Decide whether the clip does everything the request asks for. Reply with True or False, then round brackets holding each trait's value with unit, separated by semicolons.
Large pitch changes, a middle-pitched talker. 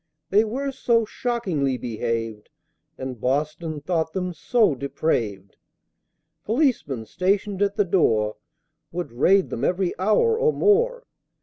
True (9.0 semitones; 180 Hz)